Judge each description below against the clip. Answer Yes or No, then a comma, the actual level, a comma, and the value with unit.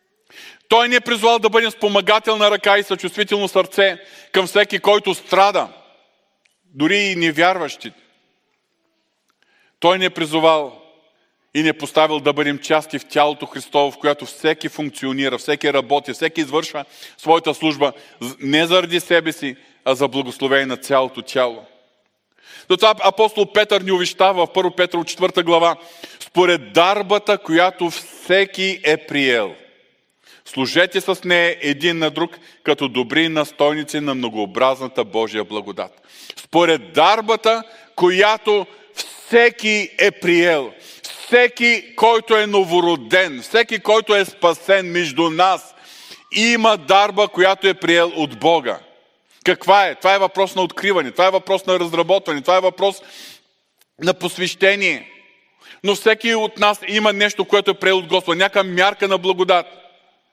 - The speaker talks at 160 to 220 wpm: No, average, 135 wpm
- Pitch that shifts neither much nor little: Yes, average, 4.4 semitones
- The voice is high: No, medium, 180 Hz